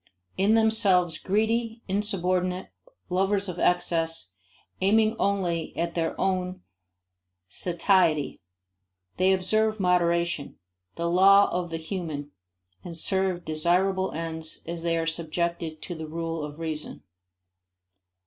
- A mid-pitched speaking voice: Yes, medium, 180 Hz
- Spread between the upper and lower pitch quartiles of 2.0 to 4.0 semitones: Yes, average, 2.7 semitones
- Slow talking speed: Yes, slow, 110 wpm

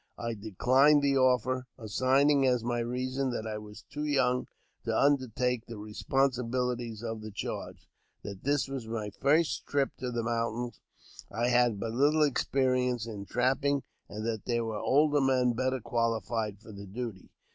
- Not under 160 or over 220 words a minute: Yes, average, 170 wpm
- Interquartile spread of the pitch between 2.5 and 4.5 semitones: Yes, average, 2.9 semitones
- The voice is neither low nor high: No, low, 125 Hz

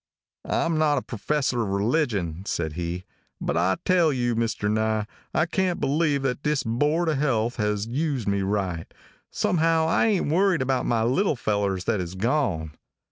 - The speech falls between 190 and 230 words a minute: No, average, 175 wpm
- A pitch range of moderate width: No, wide, 7.1 semitones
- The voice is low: Yes, low, 120 Hz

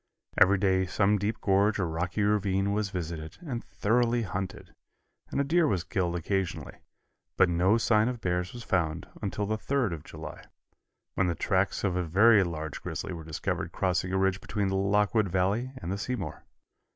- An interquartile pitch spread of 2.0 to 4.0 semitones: Yes, average, 3.0 semitones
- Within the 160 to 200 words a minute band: Yes, average, 180 wpm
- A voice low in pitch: Yes, very low, 95 Hz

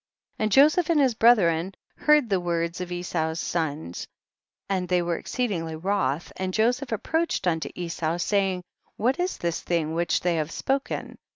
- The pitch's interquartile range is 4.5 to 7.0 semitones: Yes, wide, 5.5 semitones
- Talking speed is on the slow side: No, average, 170 wpm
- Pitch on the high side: No, medium, 180 Hz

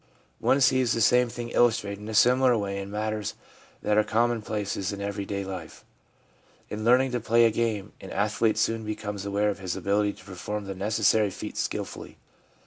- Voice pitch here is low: Yes, low, 105 Hz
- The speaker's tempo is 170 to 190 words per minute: Yes, average, 180 wpm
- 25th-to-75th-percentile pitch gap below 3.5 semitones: Yes, narrow, 2.4 semitones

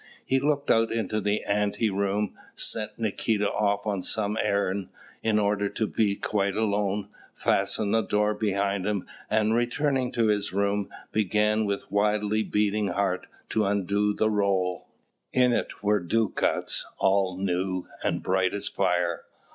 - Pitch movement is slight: Yes, narrow, 1.5 semitones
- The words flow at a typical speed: Yes, average, 145 wpm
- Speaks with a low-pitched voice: Yes, low, 105 Hz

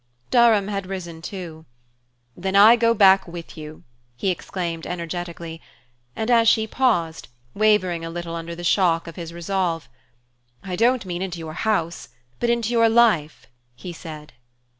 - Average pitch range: Yes, average, 4.4 semitones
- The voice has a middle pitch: Yes, medium, 180 Hz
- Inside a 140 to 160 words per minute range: Yes, average, 155 wpm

